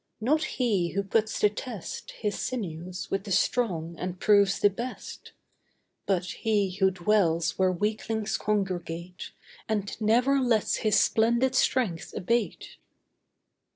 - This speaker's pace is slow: Yes, slow, 125 wpm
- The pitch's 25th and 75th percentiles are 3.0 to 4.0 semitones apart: Yes, average, 3.5 semitones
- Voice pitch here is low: No, high, 205 Hz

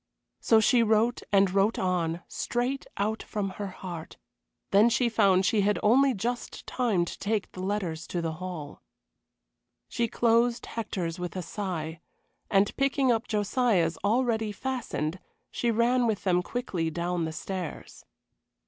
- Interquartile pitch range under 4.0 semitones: No, average, 4.6 semitones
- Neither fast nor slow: Yes, average, 150 wpm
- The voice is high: Yes, high, 205 Hz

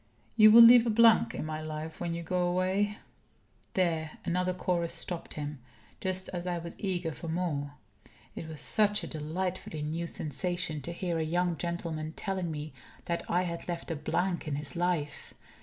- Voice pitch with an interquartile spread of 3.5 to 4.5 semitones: No, narrow, 2.6 semitones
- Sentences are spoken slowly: No, average, 185 wpm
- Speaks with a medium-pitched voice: Yes, medium, 170 Hz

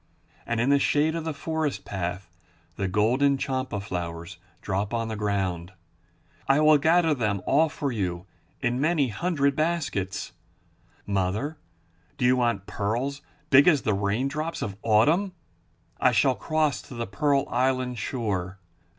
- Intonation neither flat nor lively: No, wide, 6.4 semitones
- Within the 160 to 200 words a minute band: No, average, 145 wpm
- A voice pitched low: Yes, low, 125 Hz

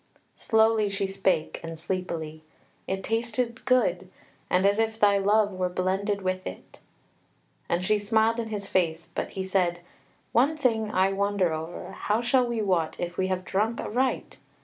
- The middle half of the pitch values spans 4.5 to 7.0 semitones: No, average, 3.3 semitones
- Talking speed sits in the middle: Yes, average, 165 wpm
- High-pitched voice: Yes, high, 200 Hz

